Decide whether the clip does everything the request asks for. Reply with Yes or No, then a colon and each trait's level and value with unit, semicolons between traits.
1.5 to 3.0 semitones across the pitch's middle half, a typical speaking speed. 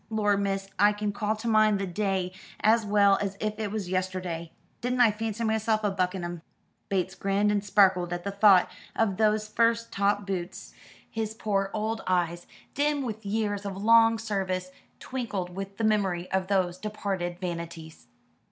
Yes: narrow, 2.6 semitones; average, 175 wpm